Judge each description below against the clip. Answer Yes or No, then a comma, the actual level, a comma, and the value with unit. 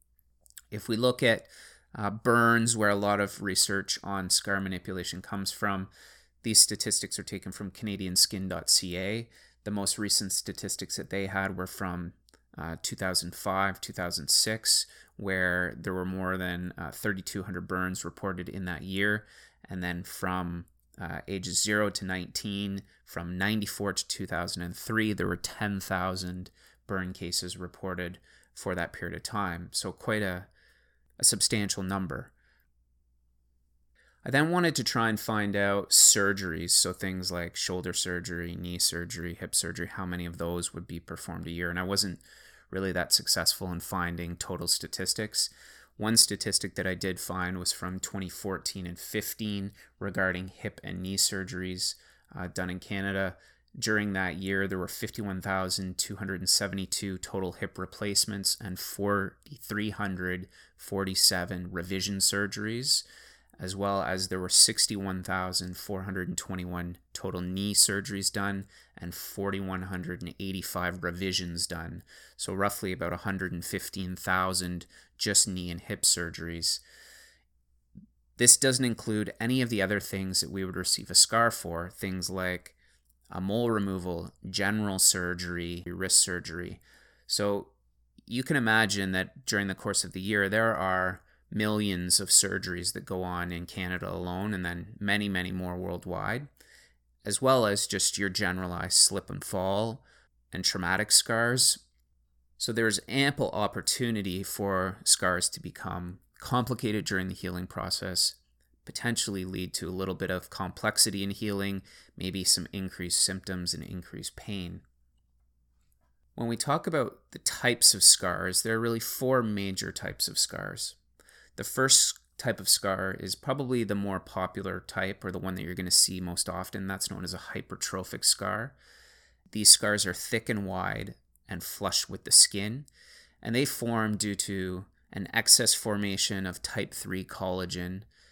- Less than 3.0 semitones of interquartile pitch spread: Yes, narrow, 2.4 semitones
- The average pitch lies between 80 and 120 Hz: Yes, very low, 95 Hz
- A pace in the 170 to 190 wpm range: No, average, 140 wpm